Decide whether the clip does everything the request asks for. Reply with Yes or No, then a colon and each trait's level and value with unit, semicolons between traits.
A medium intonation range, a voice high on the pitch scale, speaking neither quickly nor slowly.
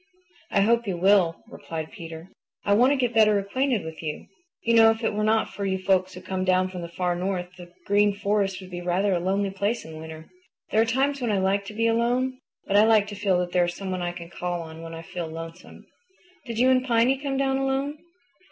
No: average, 4.4 semitones; high, 200 Hz; fast, 240 wpm